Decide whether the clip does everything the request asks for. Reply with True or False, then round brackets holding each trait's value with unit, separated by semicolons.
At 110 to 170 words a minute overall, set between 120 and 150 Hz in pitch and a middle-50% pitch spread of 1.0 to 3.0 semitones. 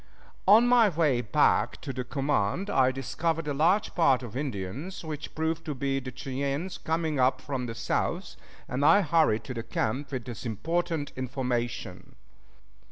False (165 wpm; 140 Hz; 4.3 semitones)